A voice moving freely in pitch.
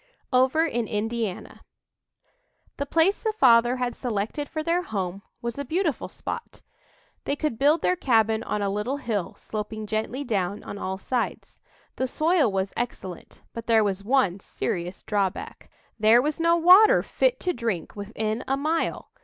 Yes: wide, 5.8 semitones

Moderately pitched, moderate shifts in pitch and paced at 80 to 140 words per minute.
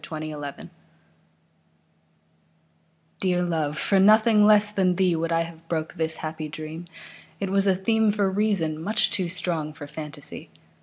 Yes: medium, 175 Hz; average, 3.9 semitones; slow, 135 wpm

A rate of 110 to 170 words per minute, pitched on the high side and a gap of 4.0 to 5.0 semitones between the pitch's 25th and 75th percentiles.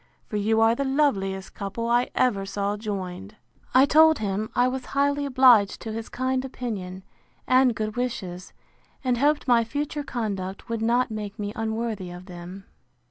Yes: average, 165 wpm; high, 225 Hz; average, 4.3 semitones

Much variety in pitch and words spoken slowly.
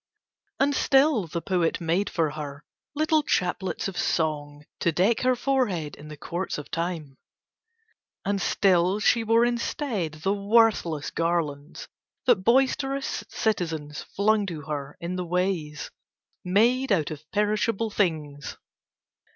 Yes: wide, 6.3 semitones; slow, 130 wpm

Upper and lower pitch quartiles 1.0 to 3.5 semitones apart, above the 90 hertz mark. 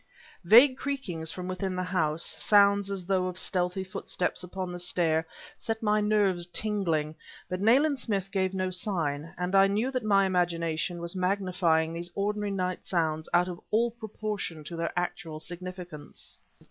Yes: average, 2.8 semitones; medium, 185 Hz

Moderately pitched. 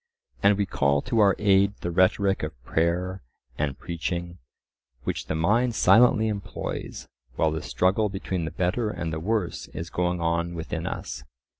No: very low, 90 Hz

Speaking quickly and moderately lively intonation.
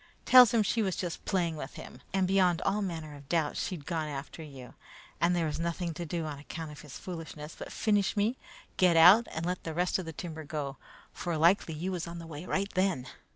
Yes: fast, 230 wpm; average, 3.3 semitones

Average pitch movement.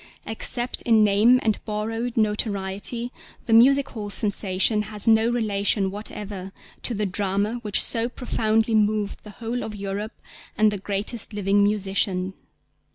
No: narrow, 2.1 semitones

